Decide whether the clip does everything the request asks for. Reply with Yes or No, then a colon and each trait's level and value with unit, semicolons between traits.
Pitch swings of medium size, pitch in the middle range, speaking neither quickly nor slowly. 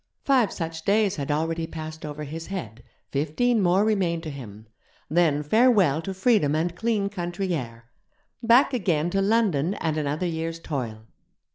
Yes: average, 4.9 semitones; medium, 165 Hz; average, 155 wpm